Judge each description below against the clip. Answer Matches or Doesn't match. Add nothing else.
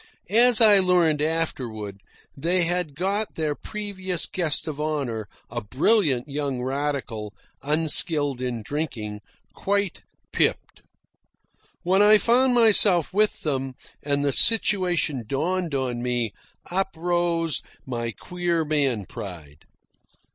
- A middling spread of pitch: Doesn't match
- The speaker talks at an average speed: Doesn't match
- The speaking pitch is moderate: Matches